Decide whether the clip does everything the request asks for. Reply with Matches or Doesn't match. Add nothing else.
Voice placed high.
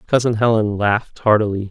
Doesn't match